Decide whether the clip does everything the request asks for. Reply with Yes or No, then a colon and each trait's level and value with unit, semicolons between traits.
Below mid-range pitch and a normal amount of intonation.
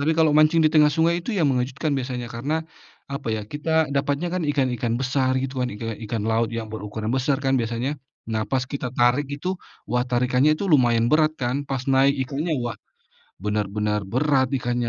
Yes: low, 130 Hz; average, 3.8 semitones